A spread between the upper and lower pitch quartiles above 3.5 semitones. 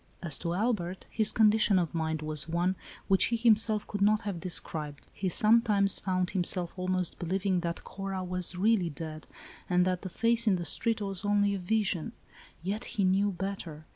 No: average, 3.1 semitones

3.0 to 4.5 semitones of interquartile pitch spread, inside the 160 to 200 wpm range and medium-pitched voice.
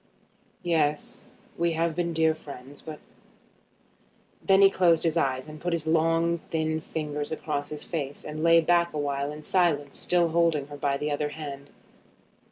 No: narrow, 2.4 semitones; average, 170 wpm; medium, 155 Hz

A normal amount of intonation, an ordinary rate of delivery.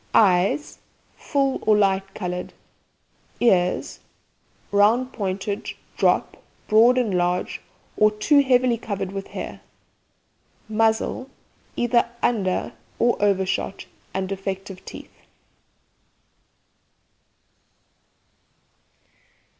No: average, 3.8 semitones; slow, 85 wpm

